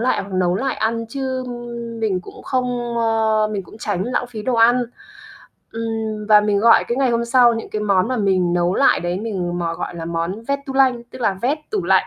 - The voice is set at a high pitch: Yes, high, 225 Hz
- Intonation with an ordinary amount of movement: Yes, average, 4.2 semitones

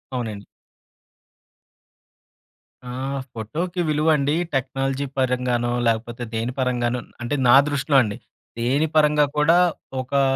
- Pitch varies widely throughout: No, average, 3.6 semitones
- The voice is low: Yes, low, 130 Hz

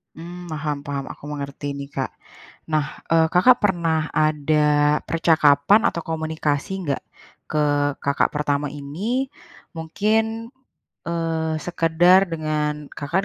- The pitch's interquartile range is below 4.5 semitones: Yes, average, 2.9 semitones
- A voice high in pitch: No, medium, 160 Hz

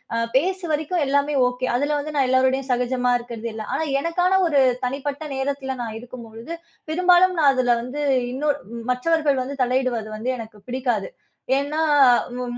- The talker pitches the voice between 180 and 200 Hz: No, very high, 265 Hz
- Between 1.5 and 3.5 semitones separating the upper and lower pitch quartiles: Yes, average, 3.2 semitones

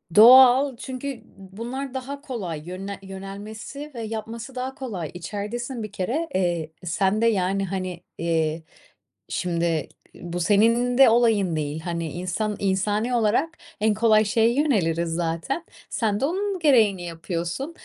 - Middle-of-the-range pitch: No, high, 210 Hz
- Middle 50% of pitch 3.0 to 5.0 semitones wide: No, wide, 5.6 semitones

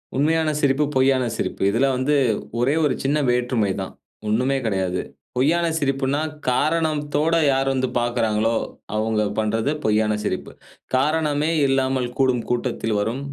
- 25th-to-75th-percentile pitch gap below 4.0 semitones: No, average, 4.4 semitones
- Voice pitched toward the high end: No, low, 130 Hz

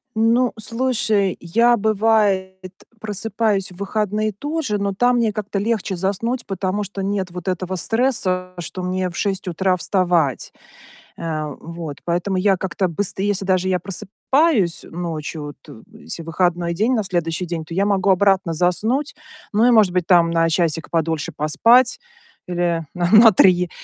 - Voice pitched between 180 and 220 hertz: Yes, high, 190 Hz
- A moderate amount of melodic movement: Yes, average, 3.6 semitones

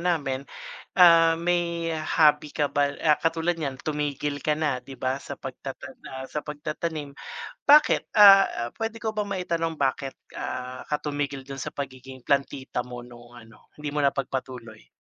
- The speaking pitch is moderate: Yes, medium, 145 Hz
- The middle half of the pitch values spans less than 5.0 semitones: Yes, average, 3.7 semitones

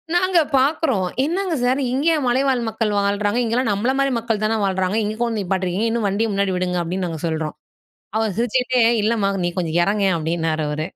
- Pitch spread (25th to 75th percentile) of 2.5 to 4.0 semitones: No, average, 5.2 semitones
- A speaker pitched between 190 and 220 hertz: Yes, high, 210 Hz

